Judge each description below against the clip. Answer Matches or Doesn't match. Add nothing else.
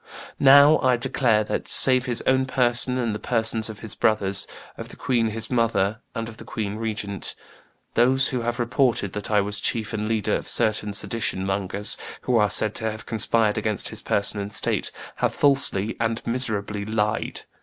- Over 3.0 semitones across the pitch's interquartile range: Doesn't match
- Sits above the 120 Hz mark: Doesn't match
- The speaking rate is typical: Matches